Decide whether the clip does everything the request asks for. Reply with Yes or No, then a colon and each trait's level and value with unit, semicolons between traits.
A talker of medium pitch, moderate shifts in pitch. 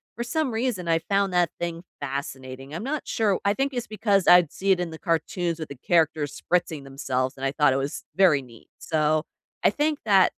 No: medium, 170 Hz; wide, 5.8 semitones